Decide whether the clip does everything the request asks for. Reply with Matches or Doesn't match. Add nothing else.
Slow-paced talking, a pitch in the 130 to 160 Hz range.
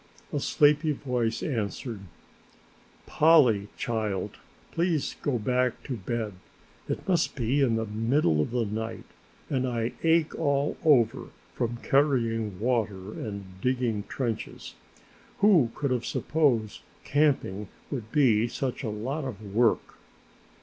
Doesn't match